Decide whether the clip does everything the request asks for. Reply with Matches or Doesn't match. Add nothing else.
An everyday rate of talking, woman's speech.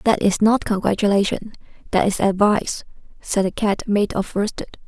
Matches